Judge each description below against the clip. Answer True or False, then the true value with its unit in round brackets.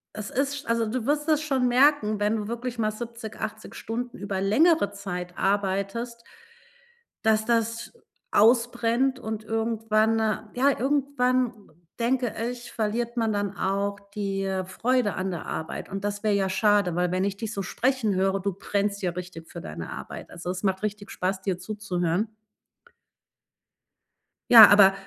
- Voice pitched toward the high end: True (215 Hz)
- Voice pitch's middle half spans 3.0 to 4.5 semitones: True (3.4 semitones)